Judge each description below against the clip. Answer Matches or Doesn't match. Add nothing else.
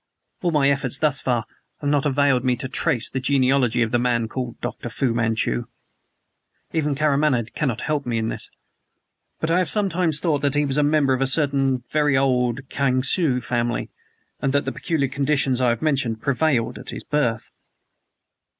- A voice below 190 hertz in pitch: Matches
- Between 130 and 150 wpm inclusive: Doesn't match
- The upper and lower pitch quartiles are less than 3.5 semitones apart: Matches